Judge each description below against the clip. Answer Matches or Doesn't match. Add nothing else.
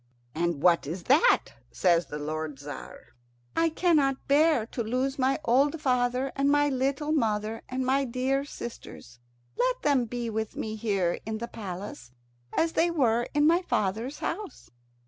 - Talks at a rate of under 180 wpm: Matches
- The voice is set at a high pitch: Matches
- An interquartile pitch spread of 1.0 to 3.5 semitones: Doesn't match